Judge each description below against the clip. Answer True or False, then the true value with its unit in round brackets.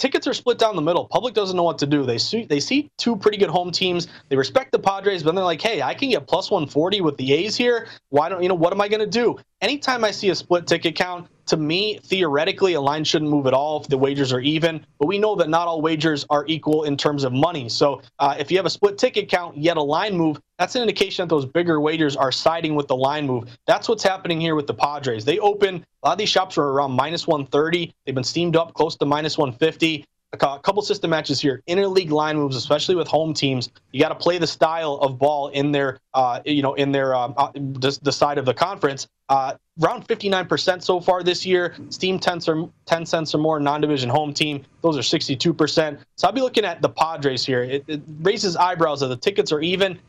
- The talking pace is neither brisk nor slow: False (255 wpm)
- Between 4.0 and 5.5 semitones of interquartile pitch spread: True (4.5 semitones)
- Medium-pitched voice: True (160 Hz)